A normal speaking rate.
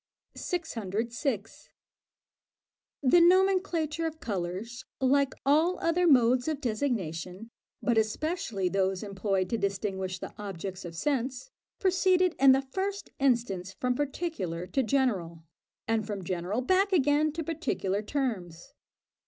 No: slow, 120 wpm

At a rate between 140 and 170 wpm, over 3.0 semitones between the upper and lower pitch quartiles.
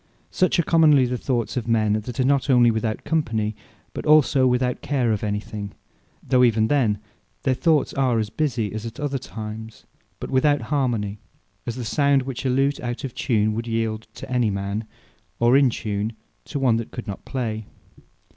No: average, 190 wpm; average, 3.6 semitones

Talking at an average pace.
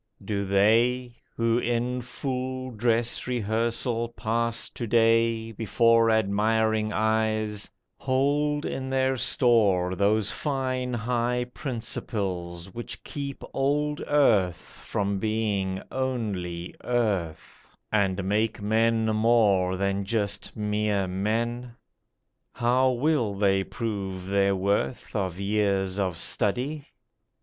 No: slow, 105 wpm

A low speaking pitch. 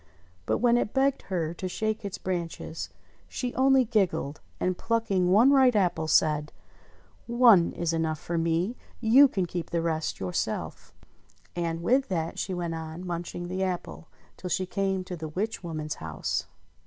No: medium, 180 Hz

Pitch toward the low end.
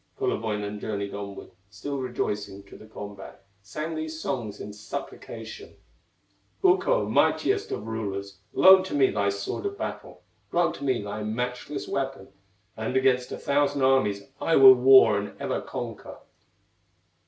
Yes: low, 120 Hz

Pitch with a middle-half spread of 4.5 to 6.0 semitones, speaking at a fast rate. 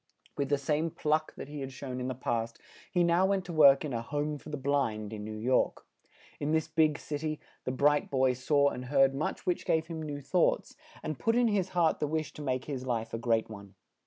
No: average, 3.5 semitones; fast, 240 wpm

